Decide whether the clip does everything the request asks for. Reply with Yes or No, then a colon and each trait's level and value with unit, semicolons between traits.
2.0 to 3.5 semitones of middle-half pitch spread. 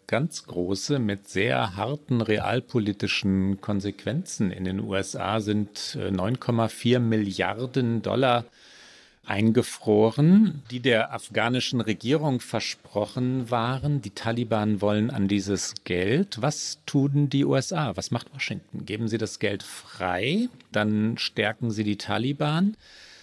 No: average, 4.0 semitones